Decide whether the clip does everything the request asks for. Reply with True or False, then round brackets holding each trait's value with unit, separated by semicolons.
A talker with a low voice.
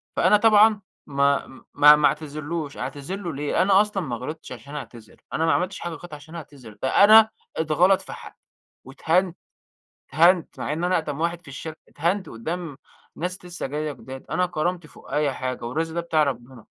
False (160 Hz)